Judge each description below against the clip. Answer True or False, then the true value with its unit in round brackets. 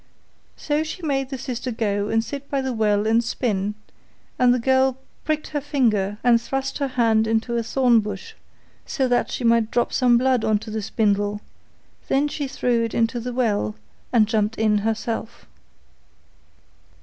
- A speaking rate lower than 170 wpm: False (175 wpm)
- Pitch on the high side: True (235 Hz)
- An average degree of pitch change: True (3.2 semitones)